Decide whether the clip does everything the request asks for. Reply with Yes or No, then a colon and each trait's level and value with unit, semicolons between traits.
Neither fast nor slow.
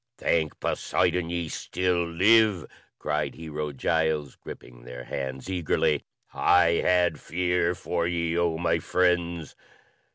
No: slow, 120 wpm